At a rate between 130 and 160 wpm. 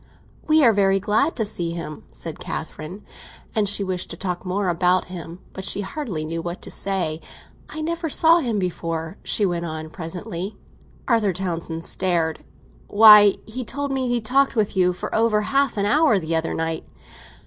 No: average, 180 wpm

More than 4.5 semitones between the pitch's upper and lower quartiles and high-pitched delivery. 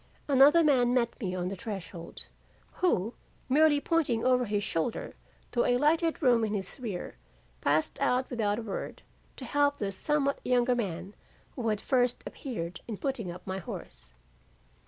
Yes: wide, 5.5 semitones; high, 240 Hz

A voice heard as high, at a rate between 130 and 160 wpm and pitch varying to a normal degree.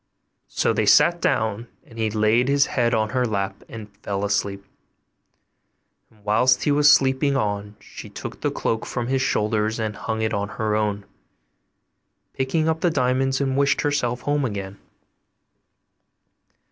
No: low, 115 Hz; average, 150 wpm; average, 4.1 semitones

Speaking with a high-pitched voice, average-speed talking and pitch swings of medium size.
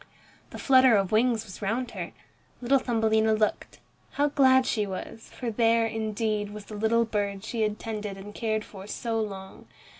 No: high, 220 Hz; average, 175 wpm; narrow, 1.9 semitones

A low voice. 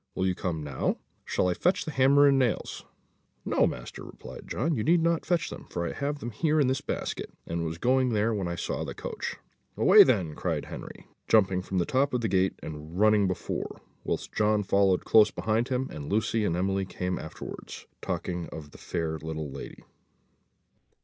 Yes: low, 100 Hz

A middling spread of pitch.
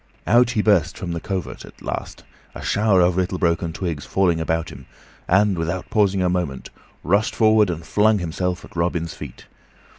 Yes: average, 3.2 semitones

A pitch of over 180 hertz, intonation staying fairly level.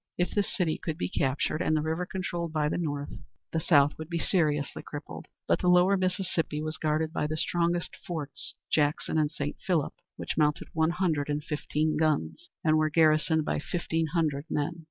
No: medium, 155 Hz; narrow, 2.3 semitones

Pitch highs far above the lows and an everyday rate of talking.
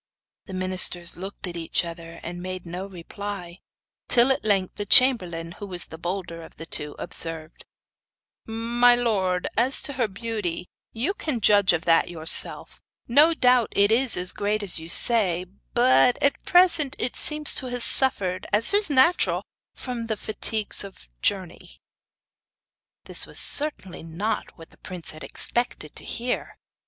Yes: wide, 5.7 semitones; average, 165 wpm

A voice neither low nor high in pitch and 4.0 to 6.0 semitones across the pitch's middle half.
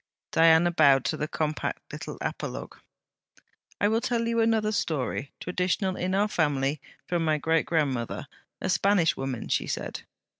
Yes: medium, 165 Hz; average, 5.1 semitones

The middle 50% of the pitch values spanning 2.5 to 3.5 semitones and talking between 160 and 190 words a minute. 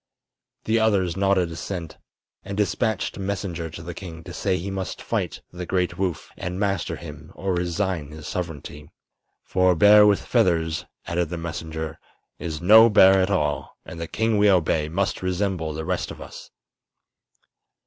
Yes: average, 3.2 semitones; average, 170 wpm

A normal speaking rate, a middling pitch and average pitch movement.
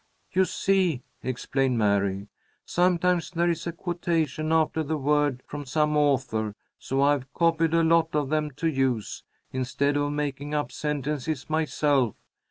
Yes: average, 145 wpm; medium, 150 Hz; average, 3.4 semitones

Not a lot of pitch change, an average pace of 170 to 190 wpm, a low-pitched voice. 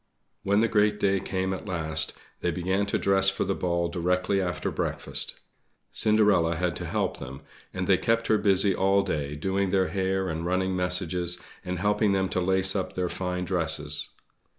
Yes: narrow, 1.9 semitones; average, 180 wpm; very low, 95 Hz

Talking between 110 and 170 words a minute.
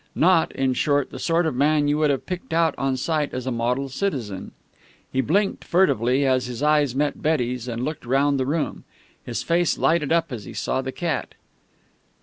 No: average, 195 wpm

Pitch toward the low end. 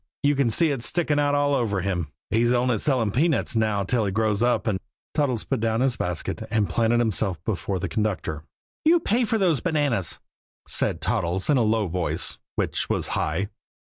Yes: low, 115 Hz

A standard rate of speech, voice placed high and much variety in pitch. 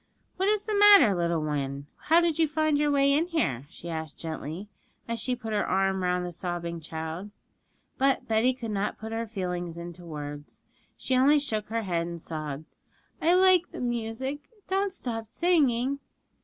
Yes: average, 180 wpm; high, 220 Hz; wide, 9.0 semitones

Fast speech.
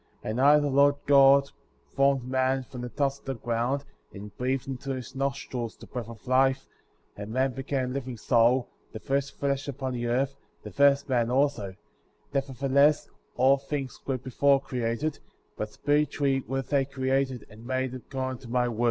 No: average, 180 wpm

